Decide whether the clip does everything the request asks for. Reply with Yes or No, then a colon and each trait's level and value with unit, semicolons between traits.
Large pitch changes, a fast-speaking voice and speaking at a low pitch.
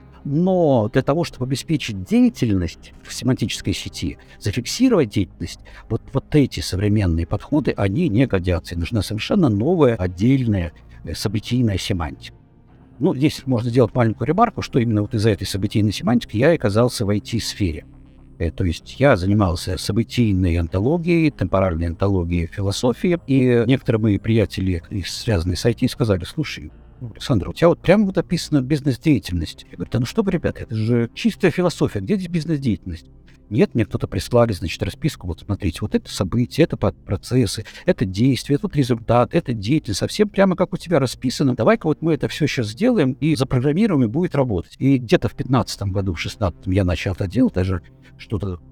Yes: wide, 6.3 semitones; fast, 165 wpm; low, 115 Hz